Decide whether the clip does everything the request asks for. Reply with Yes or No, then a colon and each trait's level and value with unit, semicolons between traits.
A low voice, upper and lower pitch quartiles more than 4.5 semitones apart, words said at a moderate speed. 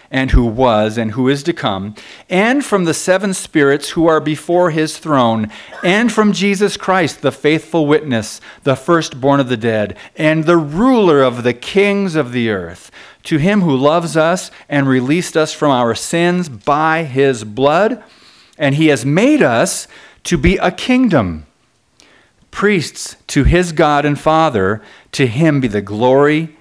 No: medium, 155 Hz; average, 5.0 semitones; average, 165 wpm